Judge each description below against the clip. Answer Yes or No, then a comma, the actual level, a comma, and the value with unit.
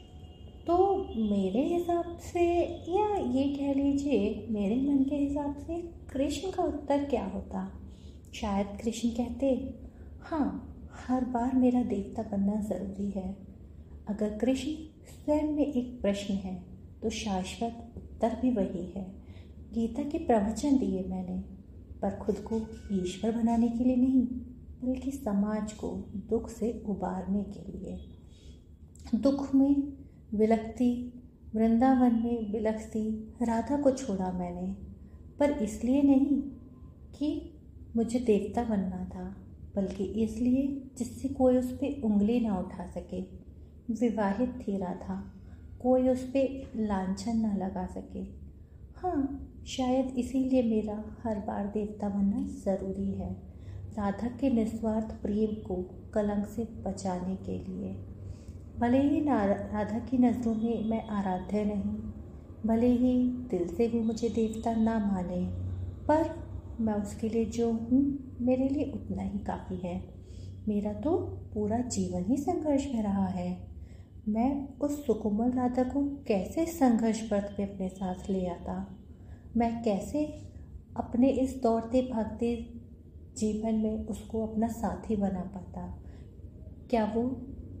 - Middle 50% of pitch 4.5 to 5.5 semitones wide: Yes, average, 5.1 semitones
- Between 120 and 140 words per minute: Yes, average, 130 wpm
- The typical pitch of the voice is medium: No, high, 220 Hz